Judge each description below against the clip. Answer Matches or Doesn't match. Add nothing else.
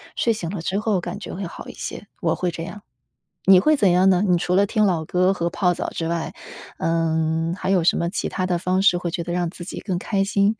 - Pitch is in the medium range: Matches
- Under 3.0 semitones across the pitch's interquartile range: Matches